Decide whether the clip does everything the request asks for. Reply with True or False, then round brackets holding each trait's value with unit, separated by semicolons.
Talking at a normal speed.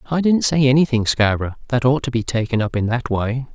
False (235 wpm)